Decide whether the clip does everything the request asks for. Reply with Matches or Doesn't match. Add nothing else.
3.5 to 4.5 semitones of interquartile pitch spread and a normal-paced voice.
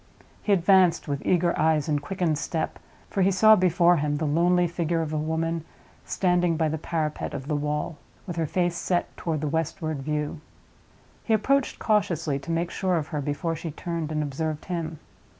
Doesn't match